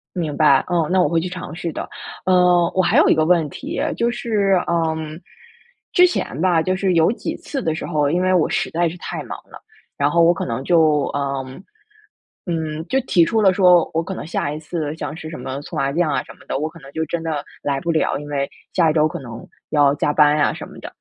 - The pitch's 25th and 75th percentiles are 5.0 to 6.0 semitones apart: No, average, 3.2 semitones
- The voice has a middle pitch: Yes, medium, 160 Hz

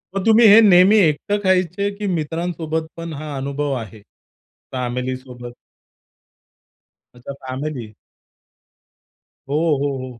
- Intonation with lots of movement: Yes, wide, 5.9 semitones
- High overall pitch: No, medium, 150 Hz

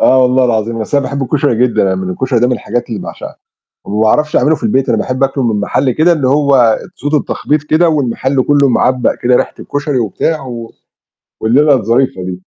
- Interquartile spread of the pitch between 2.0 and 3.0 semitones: No, average, 3.6 semitones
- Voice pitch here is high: No, low, 130 Hz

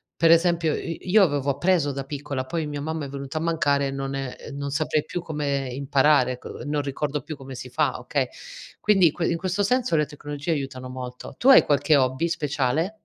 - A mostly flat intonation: No, average, 3.2 semitones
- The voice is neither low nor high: Yes, medium, 145 Hz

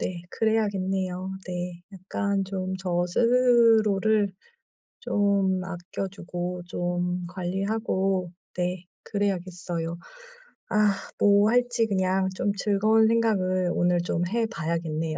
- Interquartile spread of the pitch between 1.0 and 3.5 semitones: Yes, narrow, 2.6 semitones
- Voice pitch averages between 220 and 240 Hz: No, high, 190 Hz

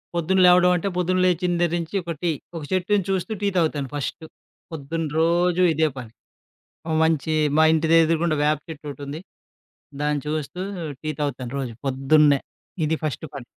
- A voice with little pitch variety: No, average, 3.0 semitones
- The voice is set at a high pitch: No, medium, 160 Hz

